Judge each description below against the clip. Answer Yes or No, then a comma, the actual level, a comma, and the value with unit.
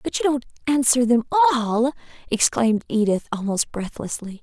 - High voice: Yes, high, 240 Hz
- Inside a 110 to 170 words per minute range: Yes, slow, 135 wpm